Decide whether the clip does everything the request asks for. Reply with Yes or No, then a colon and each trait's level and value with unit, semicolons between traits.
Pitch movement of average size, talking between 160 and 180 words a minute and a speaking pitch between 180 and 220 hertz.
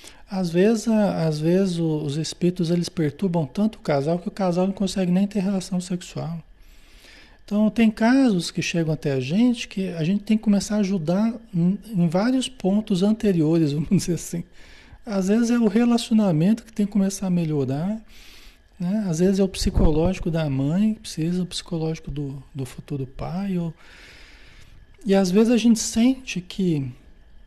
Yes: average, 4.2 semitones; average, 170 wpm; medium, 185 Hz